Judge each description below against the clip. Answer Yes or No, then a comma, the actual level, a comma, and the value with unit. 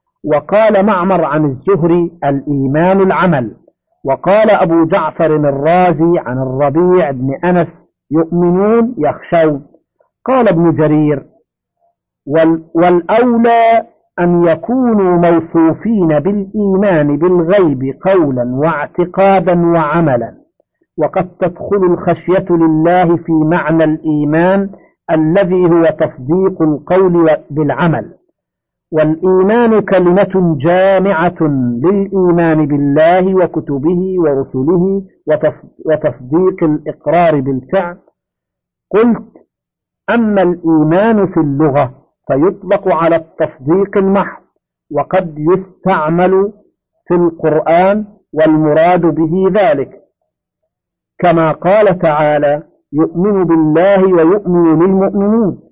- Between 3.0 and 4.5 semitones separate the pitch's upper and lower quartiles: Yes, average, 3.5 semitones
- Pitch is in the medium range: Yes, medium, 175 Hz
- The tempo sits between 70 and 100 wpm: Yes, average, 80 wpm